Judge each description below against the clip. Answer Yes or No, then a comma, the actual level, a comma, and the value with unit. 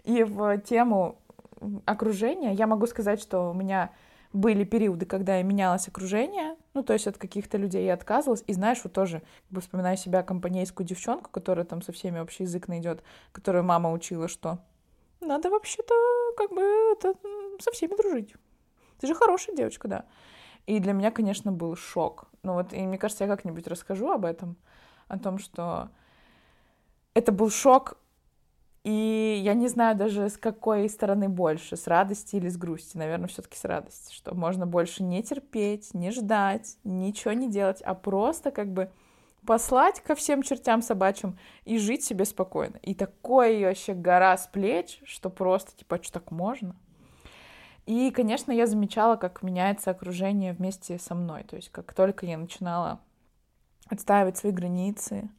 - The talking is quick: Yes, fast, 165 wpm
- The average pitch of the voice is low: No, high, 200 Hz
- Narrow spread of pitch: No, average, 3.7 semitones